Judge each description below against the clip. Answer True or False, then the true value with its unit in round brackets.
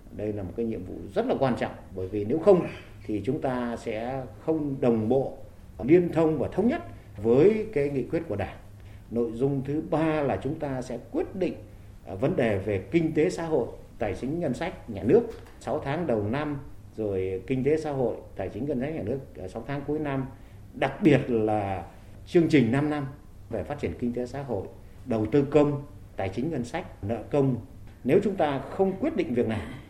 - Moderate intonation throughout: False (5.8 semitones)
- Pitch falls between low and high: False (120 Hz)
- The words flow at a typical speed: True (210 wpm)